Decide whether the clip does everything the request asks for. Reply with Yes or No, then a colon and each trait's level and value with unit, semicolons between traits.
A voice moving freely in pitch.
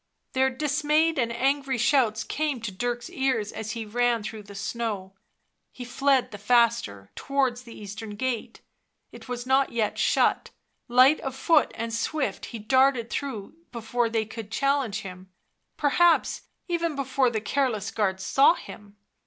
No: average, 3.8 semitones